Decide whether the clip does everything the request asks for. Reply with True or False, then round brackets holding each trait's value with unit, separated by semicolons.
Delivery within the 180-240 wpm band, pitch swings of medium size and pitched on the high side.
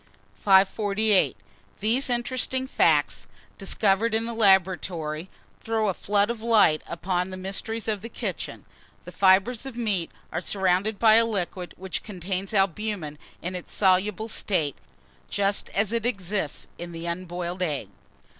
False (140 wpm; 3.4 semitones; 195 Hz)